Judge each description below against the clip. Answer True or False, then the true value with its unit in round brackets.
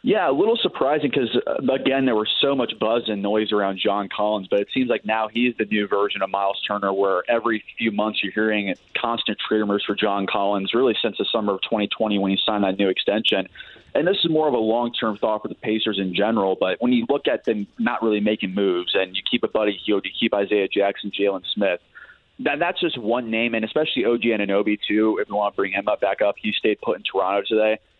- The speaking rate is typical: False (240 wpm)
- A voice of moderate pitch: False (110 Hz)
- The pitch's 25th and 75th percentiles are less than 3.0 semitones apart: True (2.5 semitones)